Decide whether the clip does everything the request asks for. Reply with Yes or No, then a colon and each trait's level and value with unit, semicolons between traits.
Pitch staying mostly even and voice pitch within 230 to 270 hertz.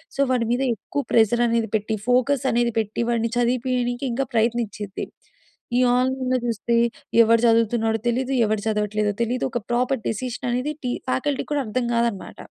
Yes: narrow, 2.2 semitones; high, 235 Hz